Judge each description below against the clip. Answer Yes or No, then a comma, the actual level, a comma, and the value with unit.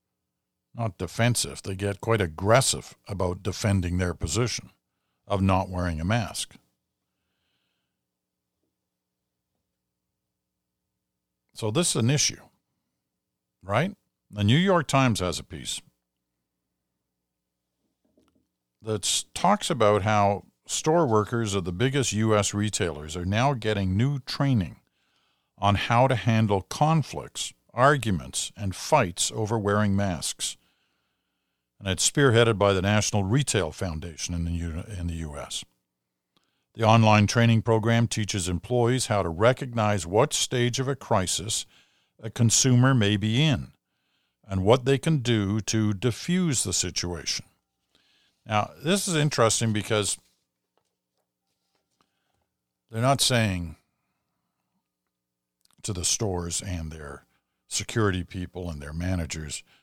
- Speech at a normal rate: No, slow, 115 wpm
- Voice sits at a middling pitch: No, low, 100 Hz